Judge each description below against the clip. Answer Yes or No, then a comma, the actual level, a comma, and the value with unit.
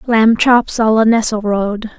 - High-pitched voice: Yes, high, 220 Hz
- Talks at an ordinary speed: Yes, average, 150 wpm